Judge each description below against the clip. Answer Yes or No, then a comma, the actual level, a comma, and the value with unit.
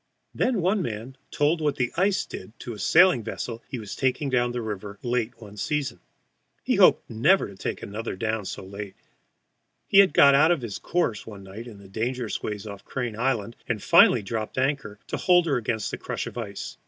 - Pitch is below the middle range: Yes, low, 120 Hz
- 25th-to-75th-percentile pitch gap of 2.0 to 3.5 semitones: No, average, 5.0 semitones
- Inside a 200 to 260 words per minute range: Yes, fast, 205 wpm